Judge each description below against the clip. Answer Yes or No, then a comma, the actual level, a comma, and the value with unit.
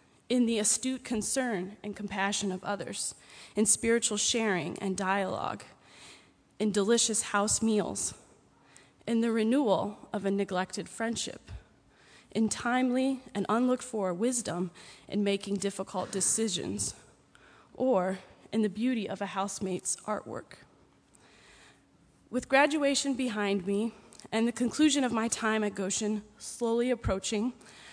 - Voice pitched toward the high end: Yes, high, 215 Hz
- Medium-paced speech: No, slow, 120 wpm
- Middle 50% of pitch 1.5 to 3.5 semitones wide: Yes, average, 2.9 semitones